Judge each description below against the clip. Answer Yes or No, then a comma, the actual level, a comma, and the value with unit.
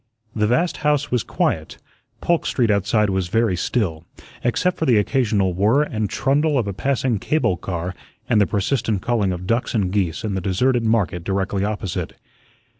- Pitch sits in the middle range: No, low, 105 Hz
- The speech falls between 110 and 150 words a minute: No, average, 175 wpm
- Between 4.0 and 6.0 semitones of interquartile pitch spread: Yes, average, 4.7 semitones